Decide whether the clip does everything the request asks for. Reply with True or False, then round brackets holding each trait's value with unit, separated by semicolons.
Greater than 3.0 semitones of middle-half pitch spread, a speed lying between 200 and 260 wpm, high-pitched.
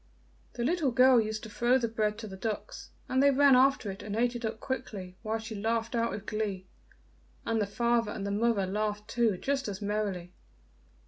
False (2.6 semitones; 205 wpm; 220 Hz)